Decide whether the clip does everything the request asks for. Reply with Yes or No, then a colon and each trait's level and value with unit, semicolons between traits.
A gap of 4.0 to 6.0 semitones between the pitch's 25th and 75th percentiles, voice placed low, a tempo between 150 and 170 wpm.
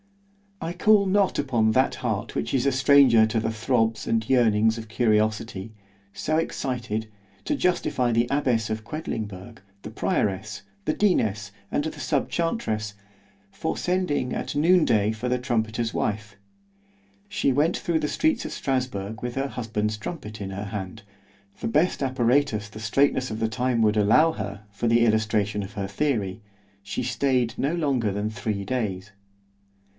Yes: average, 4.6 semitones; low, 115 Hz; average, 155 wpm